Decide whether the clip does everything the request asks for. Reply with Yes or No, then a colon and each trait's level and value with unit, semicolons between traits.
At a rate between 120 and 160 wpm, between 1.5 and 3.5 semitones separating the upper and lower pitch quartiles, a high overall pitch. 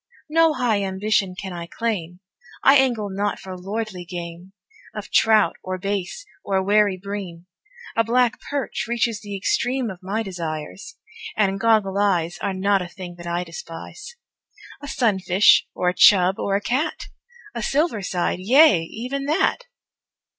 No: average, 155 wpm; average, 4.0 semitones; high, 200 Hz